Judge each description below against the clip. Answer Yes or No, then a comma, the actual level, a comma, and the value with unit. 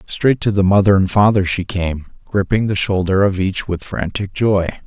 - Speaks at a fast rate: No, average, 195 wpm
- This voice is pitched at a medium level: No, very low, 95 Hz